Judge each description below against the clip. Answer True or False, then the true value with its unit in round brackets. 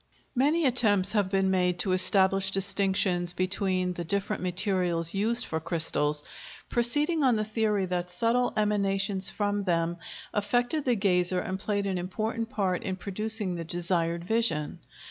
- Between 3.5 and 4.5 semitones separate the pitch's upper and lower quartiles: False (3.0 semitones)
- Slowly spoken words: False (145 wpm)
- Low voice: False (195 Hz)